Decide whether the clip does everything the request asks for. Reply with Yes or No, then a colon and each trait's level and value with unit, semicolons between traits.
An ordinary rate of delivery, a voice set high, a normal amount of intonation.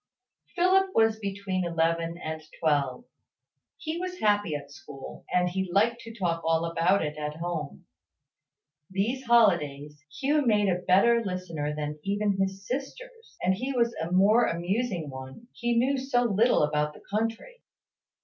No: average, 150 wpm; high, 195 Hz; wide, 6.4 semitones